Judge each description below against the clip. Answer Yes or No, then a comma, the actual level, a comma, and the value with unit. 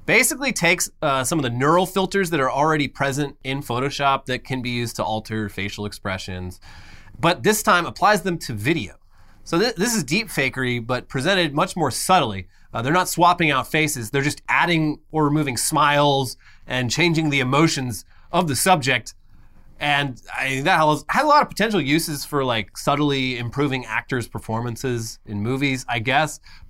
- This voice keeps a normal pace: Yes, average, 180 wpm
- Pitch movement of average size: No, wide, 6.2 semitones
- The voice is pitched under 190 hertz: Yes, medium, 140 Hz